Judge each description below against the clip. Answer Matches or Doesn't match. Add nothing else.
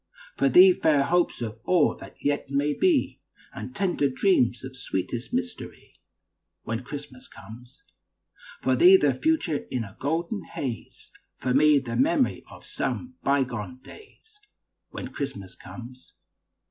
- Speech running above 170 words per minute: Doesn't match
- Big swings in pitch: Matches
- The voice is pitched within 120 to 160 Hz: Matches